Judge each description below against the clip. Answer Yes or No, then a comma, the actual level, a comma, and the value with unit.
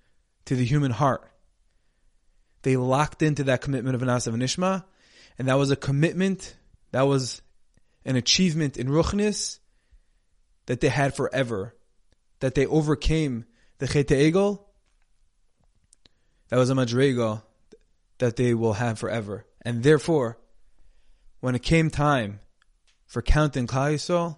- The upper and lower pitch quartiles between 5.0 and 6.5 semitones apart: No, average, 4.6 semitones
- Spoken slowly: Yes, slow, 125 wpm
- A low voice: Yes, low, 130 Hz